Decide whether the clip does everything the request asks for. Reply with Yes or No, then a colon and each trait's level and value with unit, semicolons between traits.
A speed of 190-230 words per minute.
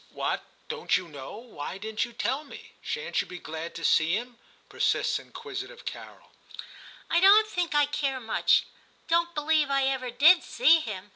Yes: average, 195 wpm